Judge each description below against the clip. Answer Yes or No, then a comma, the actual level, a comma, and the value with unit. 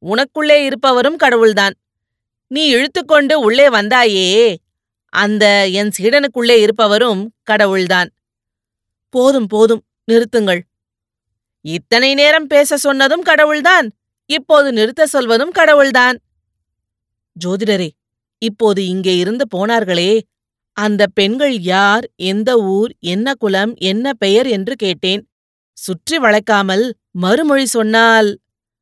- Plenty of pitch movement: Yes, wide, 5.9 semitones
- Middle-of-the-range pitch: No, high, 215 Hz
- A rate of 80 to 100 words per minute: Yes, average, 90 wpm